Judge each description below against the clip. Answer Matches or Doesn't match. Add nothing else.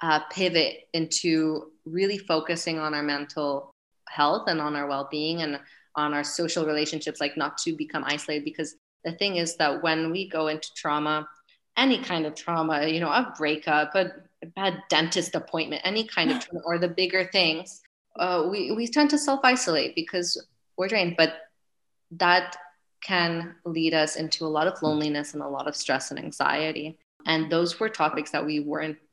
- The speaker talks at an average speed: Matches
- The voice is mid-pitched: Matches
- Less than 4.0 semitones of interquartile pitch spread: Matches